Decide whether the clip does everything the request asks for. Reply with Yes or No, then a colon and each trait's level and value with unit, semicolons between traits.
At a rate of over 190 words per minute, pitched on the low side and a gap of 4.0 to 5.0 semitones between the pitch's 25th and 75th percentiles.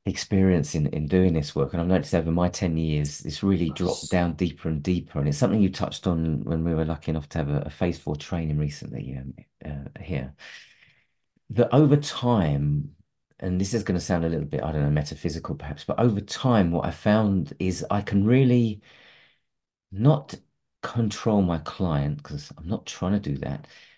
Yes: average, 200 wpm; very low, 85 Hz; average, 4.6 semitones